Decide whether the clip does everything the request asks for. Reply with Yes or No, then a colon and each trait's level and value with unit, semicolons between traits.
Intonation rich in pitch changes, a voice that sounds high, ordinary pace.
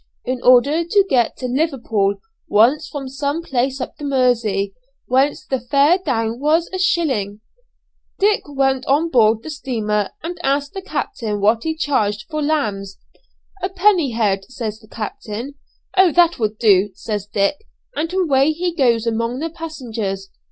Yes: wide, 6.1 semitones; very high, 260 Hz; average, 160 wpm